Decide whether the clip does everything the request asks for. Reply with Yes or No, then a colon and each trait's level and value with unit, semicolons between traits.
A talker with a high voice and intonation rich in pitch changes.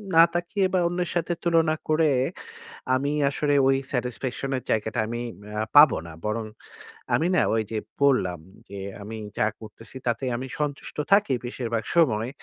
No: low, 130 Hz; wide, 5.7 semitones